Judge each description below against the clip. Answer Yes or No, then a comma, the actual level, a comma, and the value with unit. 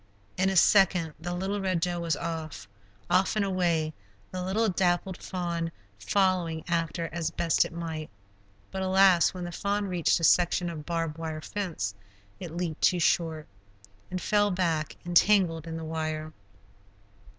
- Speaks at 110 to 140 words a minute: No, average, 155 wpm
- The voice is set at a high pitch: No, medium, 170 Hz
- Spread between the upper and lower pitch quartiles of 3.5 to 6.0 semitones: No, narrow, 2.4 semitones